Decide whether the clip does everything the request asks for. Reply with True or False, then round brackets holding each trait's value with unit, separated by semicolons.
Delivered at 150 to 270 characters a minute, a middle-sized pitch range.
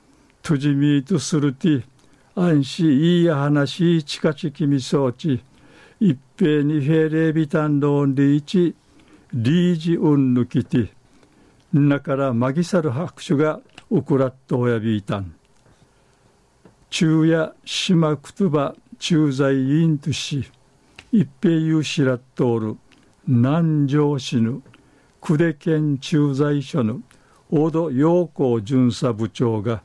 True (265 characters per minute; 3.5 semitones)